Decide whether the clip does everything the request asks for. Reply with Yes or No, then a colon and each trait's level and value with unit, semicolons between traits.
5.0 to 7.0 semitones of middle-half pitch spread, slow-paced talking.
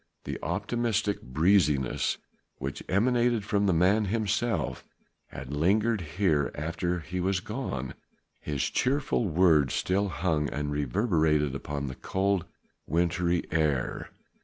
Yes: wide, 5.6 semitones; slow, 115 wpm